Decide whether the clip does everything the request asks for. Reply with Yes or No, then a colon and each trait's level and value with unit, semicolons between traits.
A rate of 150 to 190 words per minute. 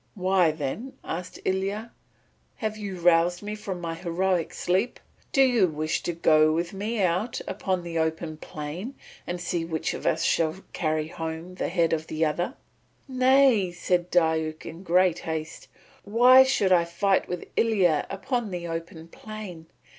Yes: average, 160 wpm